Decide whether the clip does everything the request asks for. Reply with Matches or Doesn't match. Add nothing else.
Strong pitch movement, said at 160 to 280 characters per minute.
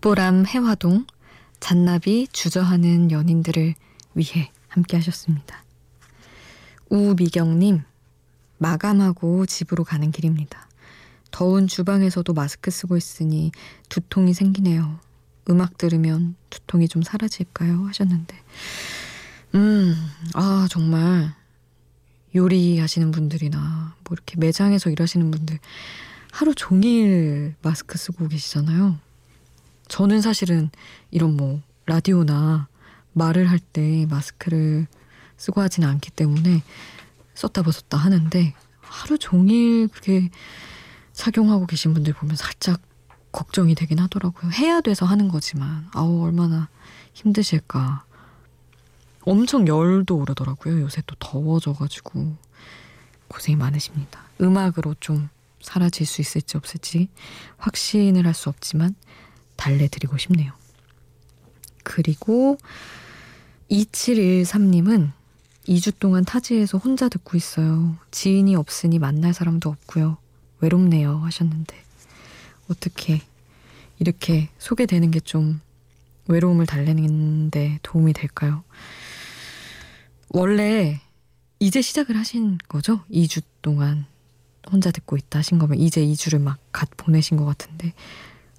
Doesn't match